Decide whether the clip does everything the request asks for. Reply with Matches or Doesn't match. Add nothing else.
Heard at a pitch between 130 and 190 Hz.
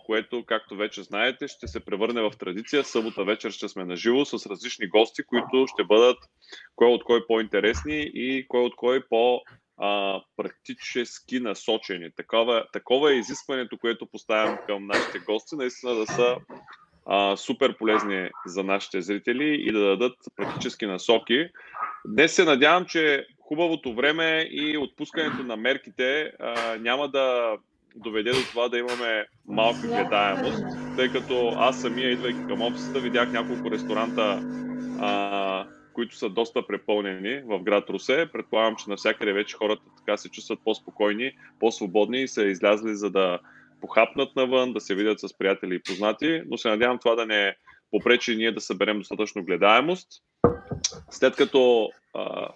Doesn't match